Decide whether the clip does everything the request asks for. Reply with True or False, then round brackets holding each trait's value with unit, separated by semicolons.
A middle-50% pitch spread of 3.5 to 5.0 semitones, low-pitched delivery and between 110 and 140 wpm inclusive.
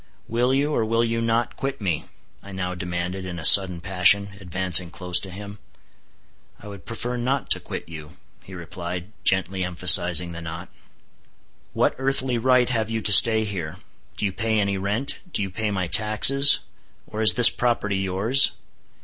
False (4.0 semitones; 100 Hz; 175 wpm)